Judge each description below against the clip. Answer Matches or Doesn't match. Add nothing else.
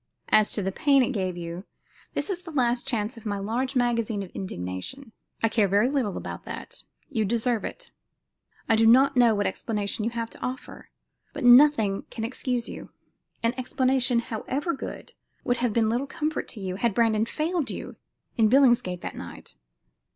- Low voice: Doesn't match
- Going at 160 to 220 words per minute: Matches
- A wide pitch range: Doesn't match